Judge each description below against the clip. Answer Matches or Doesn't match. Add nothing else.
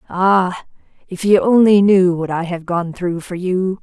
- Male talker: Doesn't match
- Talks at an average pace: Matches